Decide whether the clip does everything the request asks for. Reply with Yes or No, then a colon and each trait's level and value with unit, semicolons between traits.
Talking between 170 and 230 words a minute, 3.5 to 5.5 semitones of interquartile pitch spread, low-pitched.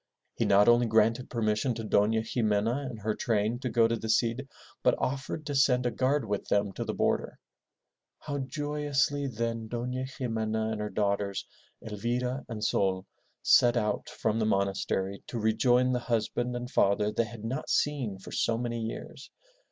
No: average, 175 wpm; average, 2.9 semitones; low, 115 Hz